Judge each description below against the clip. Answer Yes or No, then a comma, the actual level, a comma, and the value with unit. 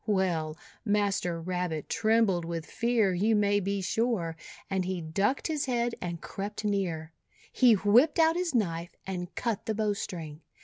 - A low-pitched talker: No, high, 200 Hz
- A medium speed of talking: Yes, average, 150 wpm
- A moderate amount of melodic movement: Yes, average, 4.4 semitones